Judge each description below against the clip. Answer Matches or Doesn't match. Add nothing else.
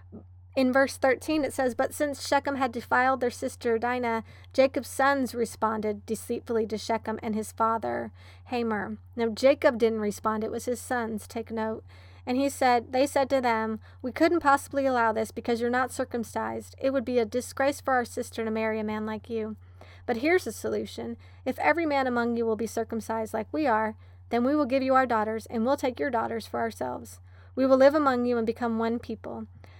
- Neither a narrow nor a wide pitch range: Matches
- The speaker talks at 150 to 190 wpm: Doesn't match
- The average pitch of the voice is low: Doesn't match